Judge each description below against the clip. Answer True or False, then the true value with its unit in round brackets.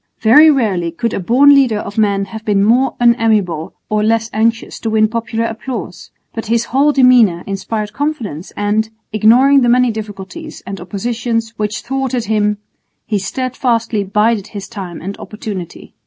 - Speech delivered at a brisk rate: False (155 wpm)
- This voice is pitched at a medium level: False (220 Hz)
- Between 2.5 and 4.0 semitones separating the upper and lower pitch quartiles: True (2.8 semitones)